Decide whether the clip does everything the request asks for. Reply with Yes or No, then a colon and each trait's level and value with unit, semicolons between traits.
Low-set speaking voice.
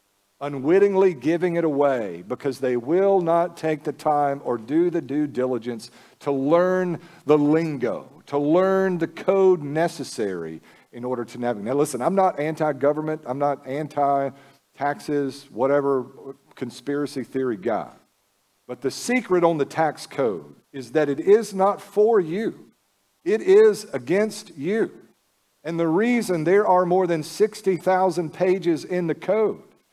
No: medium, 155 Hz